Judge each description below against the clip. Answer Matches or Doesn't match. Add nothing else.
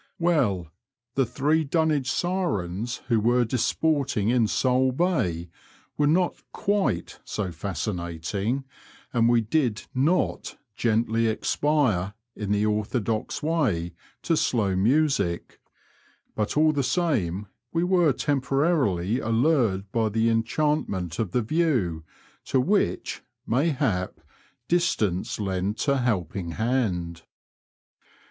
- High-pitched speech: Doesn't match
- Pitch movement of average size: Doesn't match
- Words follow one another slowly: Matches